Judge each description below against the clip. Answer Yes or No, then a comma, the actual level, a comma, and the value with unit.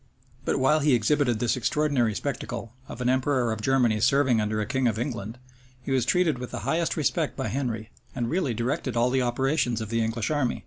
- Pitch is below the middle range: Yes, low, 125 Hz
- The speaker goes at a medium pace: No, fast, 210 wpm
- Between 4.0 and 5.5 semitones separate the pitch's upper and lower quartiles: No, average, 3.3 semitones